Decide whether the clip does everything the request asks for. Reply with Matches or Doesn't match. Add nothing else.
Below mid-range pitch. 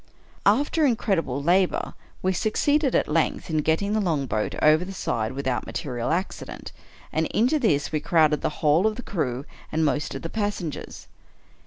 Doesn't match